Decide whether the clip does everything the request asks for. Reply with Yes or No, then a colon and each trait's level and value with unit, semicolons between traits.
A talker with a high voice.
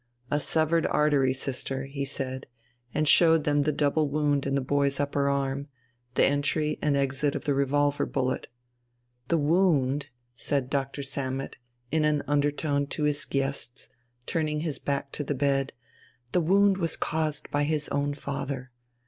No: medium, 145 Hz